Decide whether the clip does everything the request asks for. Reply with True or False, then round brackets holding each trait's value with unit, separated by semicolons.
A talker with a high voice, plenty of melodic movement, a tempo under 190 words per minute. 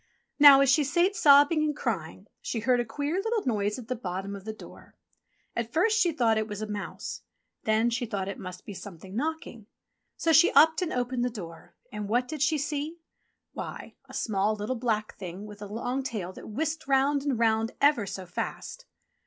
False (235 Hz; 5.8 semitones; 200 wpm)